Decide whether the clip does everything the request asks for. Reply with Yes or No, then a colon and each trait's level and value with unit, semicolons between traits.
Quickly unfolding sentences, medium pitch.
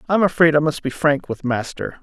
Yes: fast, 235 wpm; medium, 150 Hz